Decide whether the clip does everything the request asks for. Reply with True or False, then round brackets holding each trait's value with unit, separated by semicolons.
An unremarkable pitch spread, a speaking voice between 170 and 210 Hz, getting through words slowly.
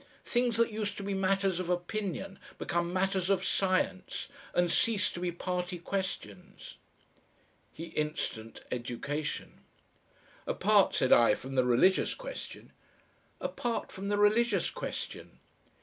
True (3.0 semitones; 185 Hz; 125 wpm)